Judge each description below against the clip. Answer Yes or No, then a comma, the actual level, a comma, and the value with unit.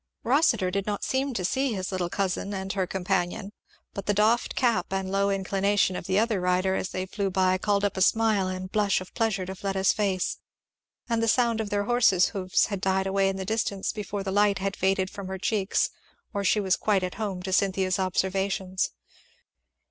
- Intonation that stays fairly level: Yes, narrow, 1.6 semitones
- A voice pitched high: Yes, high, 195 Hz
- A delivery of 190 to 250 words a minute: Yes, fast, 205 wpm